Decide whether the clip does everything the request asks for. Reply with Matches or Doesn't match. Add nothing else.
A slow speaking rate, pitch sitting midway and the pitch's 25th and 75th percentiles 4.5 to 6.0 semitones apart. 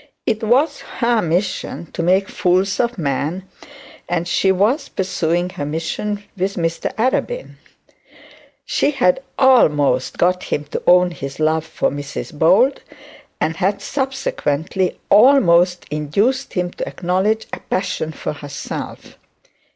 Matches